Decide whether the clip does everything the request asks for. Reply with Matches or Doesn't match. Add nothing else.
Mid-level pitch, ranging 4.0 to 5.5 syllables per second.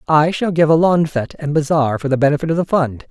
Doesn't match